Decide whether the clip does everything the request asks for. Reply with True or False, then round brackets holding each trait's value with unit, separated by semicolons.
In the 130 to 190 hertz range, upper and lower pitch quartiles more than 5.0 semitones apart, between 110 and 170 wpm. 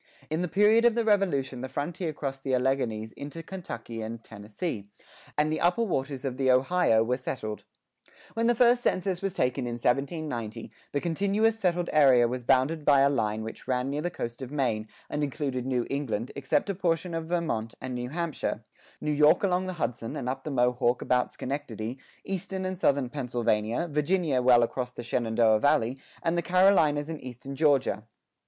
False (140 Hz; 5.6 semitones; 185 wpm)